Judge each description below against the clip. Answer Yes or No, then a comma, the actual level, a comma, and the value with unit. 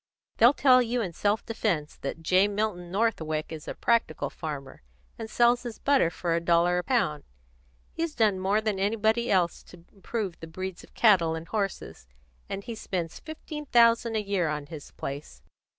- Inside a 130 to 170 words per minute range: No, average, 180 wpm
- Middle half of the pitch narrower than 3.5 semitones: No, wide, 5.5 semitones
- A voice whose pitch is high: Yes, high, 195 Hz